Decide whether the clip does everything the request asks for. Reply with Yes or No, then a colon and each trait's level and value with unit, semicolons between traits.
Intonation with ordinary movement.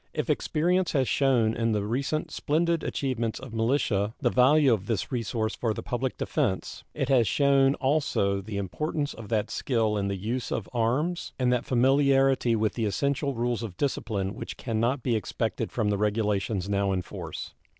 Yes: average, 4.3 semitones